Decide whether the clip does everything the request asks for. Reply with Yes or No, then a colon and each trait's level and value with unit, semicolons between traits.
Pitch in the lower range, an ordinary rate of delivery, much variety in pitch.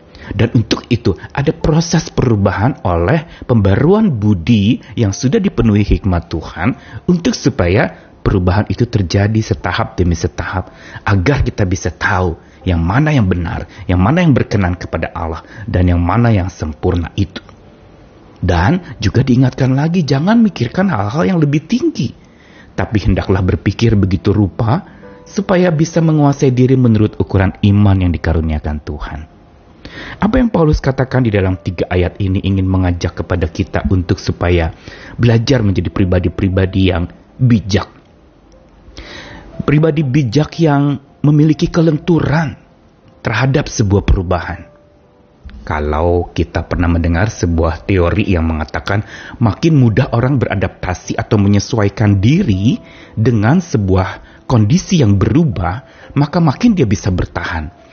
Yes: low, 105 Hz; average, 125 wpm; wide, 6.4 semitones